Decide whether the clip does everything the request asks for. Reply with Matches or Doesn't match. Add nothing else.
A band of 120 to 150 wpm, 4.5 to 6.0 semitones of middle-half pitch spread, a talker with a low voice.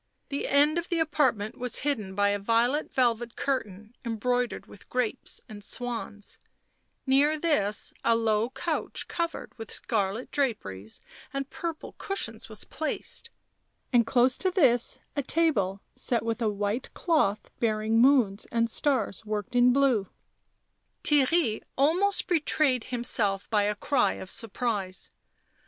Doesn't match